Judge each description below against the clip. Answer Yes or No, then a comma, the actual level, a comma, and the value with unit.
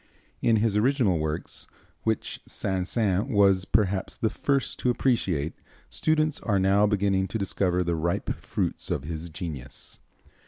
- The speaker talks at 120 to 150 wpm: Yes, average, 145 wpm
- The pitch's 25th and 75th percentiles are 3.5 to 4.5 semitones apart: Yes, average, 4.2 semitones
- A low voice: Yes, very low, 95 Hz